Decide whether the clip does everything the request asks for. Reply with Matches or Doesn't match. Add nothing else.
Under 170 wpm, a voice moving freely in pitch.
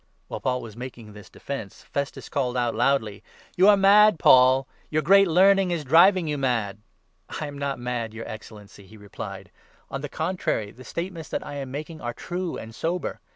Doesn't match